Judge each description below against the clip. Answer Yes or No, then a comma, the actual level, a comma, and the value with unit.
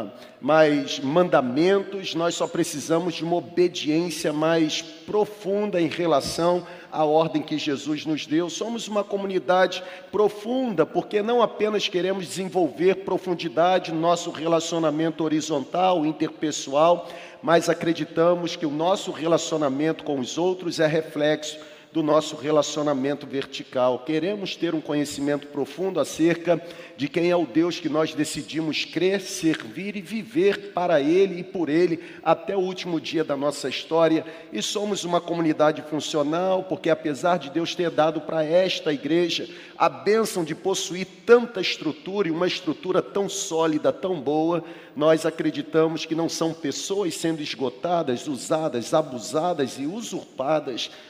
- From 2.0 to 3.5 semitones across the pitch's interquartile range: Yes, average, 2.9 semitones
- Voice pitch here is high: No, medium, 165 Hz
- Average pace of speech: Yes, average, 135 wpm